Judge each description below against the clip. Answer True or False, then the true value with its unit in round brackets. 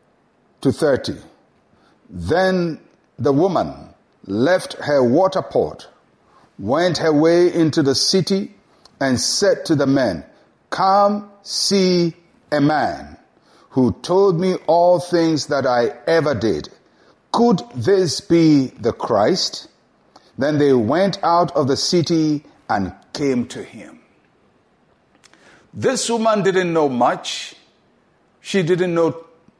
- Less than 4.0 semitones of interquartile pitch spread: False (4.3 semitones)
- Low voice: False (165 Hz)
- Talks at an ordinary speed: False (115 wpm)